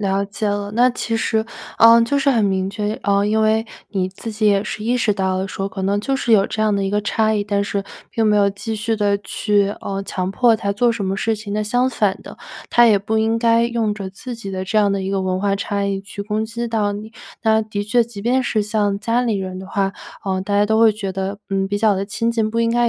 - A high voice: Yes, high, 210 Hz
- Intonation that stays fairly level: Yes, narrow, 2.2 semitones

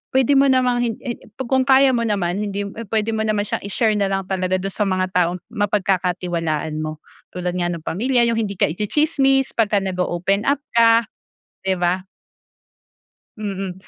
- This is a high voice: Yes, high, 200 Hz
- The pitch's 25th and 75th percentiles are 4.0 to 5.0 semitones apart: Yes, average, 4.3 semitones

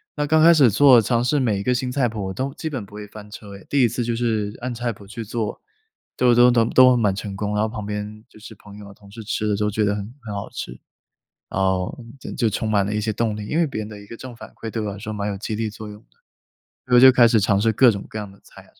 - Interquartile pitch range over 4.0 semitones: No, average, 2.8 semitones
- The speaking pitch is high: No, low, 110 Hz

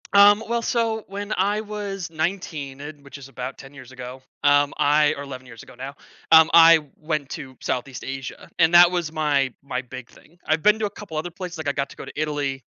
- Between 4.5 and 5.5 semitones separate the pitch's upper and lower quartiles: Yes, average, 5.0 semitones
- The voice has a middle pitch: Yes, medium, 155 Hz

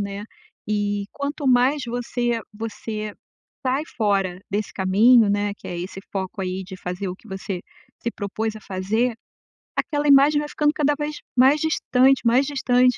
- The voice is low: No, high, 225 Hz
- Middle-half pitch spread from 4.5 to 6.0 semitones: Yes, average, 5.0 semitones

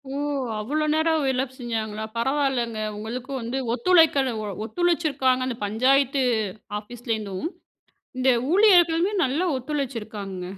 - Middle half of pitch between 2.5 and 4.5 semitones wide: No, average, 5.1 semitones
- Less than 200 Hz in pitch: No, very high, 260 Hz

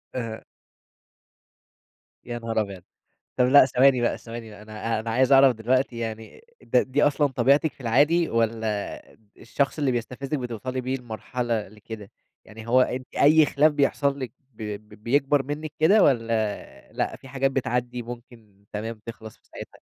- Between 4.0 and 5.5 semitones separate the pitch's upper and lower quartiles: No, average, 3.3 semitones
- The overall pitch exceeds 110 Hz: Yes, low, 120 Hz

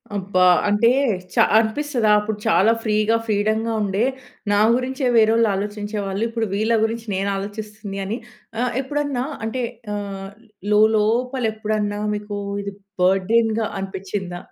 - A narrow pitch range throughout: Yes, narrow, 2.1 semitones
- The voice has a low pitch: No, high, 215 Hz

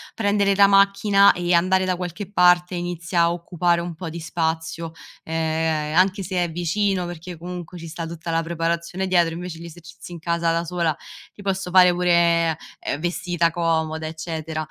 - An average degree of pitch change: No, narrow, 1.6 semitones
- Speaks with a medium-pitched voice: Yes, medium, 170 Hz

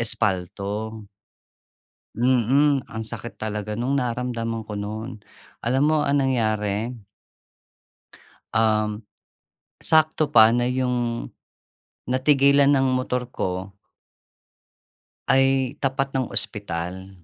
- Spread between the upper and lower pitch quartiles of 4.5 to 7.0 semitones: No, average, 3.7 semitones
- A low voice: Yes, low, 120 Hz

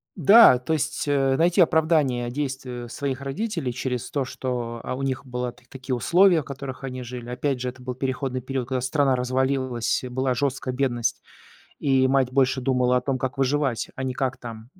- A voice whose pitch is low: Yes, low, 130 Hz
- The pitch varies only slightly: Yes, narrow, 1.7 semitones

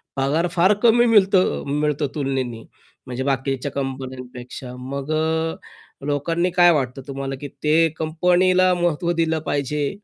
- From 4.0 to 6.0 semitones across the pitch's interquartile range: Yes, average, 4.3 semitones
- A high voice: No, medium, 150 Hz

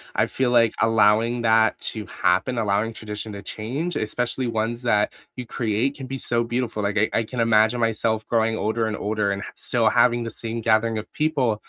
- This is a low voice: Yes, low, 115 Hz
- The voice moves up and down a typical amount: No, narrow, 1.9 semitones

